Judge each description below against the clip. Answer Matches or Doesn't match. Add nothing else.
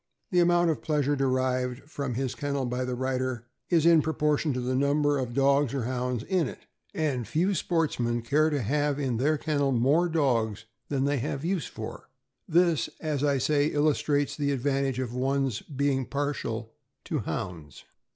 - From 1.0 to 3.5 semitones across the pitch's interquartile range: Matches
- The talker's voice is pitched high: Doesn't match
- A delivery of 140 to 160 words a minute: Doesn't match